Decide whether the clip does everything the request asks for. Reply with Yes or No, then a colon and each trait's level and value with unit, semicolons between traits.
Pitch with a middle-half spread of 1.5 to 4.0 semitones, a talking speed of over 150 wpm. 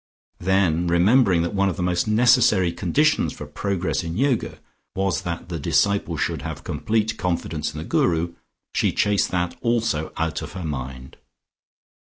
Yes: average, 3.7 semitones; average, 160 wpm